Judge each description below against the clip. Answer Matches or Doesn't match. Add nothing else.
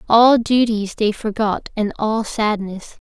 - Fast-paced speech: Doesn't match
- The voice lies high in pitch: Matches